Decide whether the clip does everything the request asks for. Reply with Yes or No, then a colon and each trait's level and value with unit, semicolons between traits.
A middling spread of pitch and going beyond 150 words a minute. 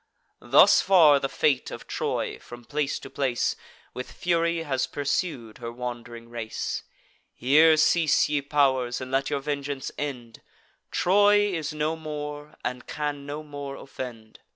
No: average, 3.3 semitones; average, 145 wpm